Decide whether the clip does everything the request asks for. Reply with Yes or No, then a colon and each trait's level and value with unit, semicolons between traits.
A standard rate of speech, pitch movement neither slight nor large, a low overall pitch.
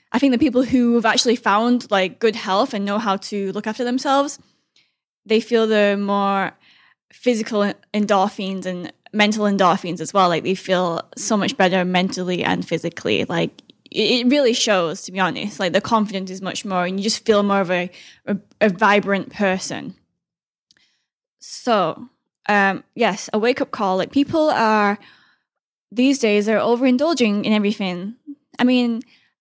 No: average, 160 wpm; average, 3.6 semitones; high, 210 Hz